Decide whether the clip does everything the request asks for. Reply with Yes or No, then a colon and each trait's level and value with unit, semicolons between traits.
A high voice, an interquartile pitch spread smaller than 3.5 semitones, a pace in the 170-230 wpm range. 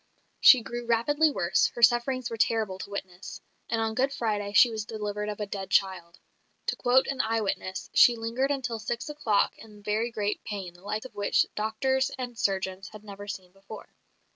Yes: high, 220 Hz; average, 3.1 semitones; average, 190 wpm